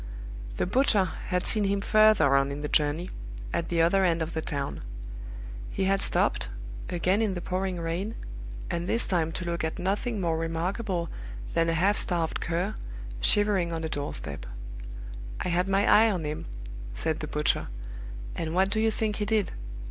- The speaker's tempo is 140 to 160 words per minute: No, average, 180 wpm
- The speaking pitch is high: No, medium, 180 Hz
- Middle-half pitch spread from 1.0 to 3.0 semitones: No, average, 3.5 semitones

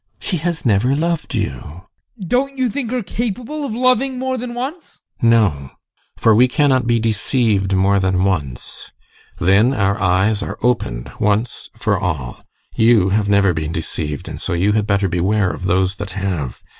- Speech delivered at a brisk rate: No, average, 175 wpm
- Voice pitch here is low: Yes, low, 105 Hz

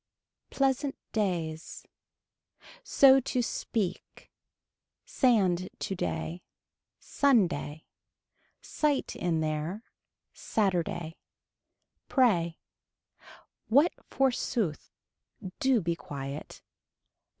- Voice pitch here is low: No, high, 190 Hz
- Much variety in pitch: Yes, wide, 7.8 semitones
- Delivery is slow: Yes, slow, 60 wpm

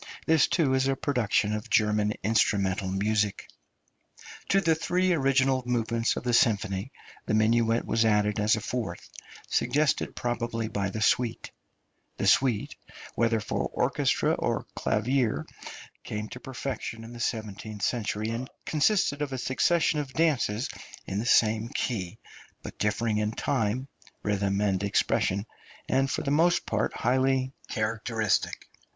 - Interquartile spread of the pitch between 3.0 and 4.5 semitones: Yes, average, 3.9 semitones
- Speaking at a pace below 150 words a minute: Yes, average, 140 wpm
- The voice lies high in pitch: No, low, 115 Hz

